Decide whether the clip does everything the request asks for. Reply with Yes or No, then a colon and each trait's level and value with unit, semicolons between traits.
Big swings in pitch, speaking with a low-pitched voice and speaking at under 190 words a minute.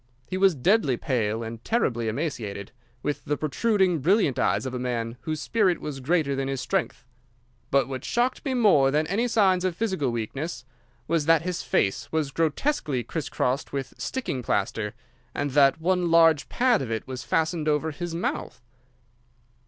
No: wide, 5.8 semitones; medium, 150 Hz; average, 170 wpm